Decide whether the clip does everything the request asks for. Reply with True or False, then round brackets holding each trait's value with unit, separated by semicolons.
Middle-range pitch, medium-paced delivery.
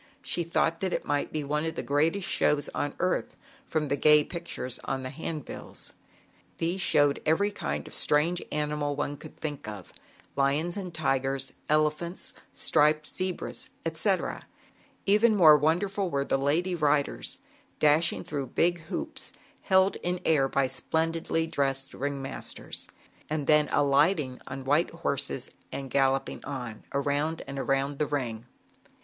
True (150 Hz; 145 wpm)